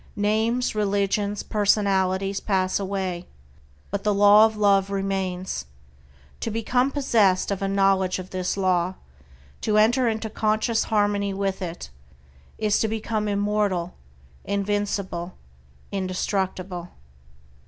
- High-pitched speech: Yes, high, 200 Hz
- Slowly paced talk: Yes, slow, 110 wpm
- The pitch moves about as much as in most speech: No, narrow, 2.1 semitones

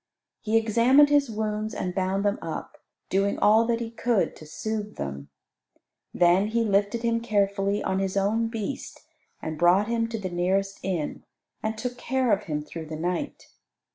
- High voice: Yes, high, 205 Hz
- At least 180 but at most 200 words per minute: No, average, 170 wpm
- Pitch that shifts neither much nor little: Yes, average, 3.4 semitones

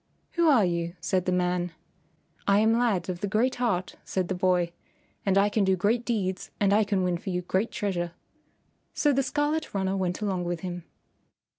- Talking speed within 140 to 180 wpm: No, average, 195 wpm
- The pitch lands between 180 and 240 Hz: Yes, high, 190 Hz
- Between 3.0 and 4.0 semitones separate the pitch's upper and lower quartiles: Yes, average, 3.5 semitones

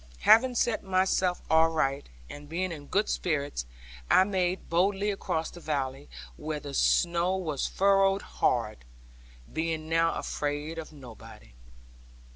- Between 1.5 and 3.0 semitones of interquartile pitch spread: No, average, 4.3 semitones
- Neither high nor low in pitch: Yes, medium, 165 Hz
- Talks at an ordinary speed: No, slow, 125 wpm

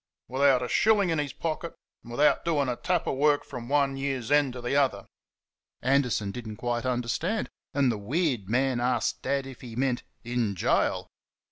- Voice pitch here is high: No, low, 130 Hz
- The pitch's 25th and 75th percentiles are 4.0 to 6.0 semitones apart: No, average, 3.0 semitones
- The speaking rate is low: No, average, 190 wpm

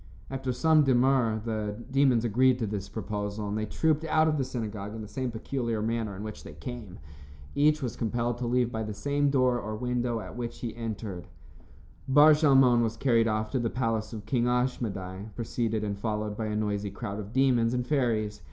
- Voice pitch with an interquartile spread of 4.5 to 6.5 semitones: No, average, 3.0 semitones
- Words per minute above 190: Yes, average, 200 wpm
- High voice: No, low, 115 Hz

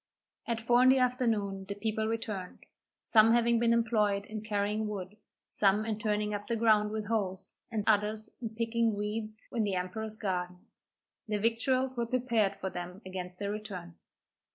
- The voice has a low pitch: No, high, 215 Hz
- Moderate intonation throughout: No, narrow, 2.2 semitones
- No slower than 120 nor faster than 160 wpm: No, average, 170 wpm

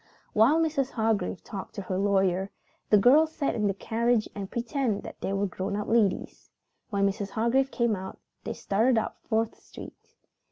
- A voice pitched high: Yes, high, 220 Hz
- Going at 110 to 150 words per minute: No, average, 175 wpm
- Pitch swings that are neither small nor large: Yes, average, 3.4 semitones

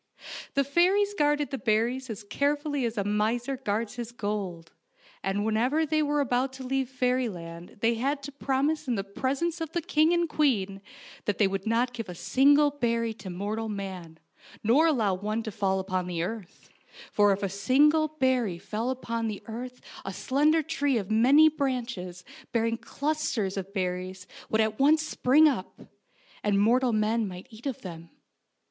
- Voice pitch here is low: No, high, 230 Hz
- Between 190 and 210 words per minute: No, average, 175 wpm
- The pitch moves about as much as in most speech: No, wide, 5.7 semitones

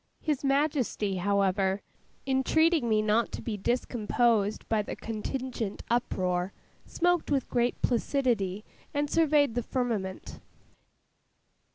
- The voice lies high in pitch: Yes, high, 235 Hz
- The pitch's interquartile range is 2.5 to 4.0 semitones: No, average, 5.0 semitones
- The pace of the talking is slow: Yes, slow, 105 wpm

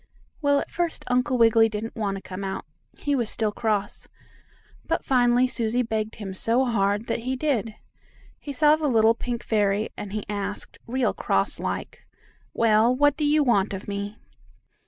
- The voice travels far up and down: No, average, 3.5 semitones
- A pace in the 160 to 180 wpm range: Yes, average, 175 wpm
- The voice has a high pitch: Yes, high, 225 Hz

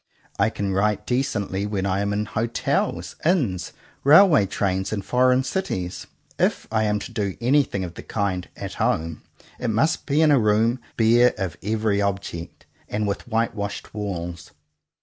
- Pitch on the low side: Yes, low, 105 Hz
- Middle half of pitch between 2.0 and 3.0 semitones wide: No, average, 3.6 semitones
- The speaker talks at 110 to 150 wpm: No, average, 165 wpm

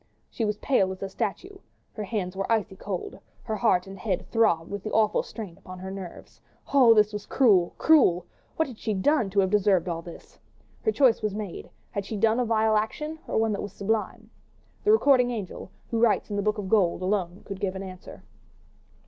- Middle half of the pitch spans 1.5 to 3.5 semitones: Yes, average, 3.0 semitones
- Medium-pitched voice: No, high, 210 Hz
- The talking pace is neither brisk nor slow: No, fast, 210 wpm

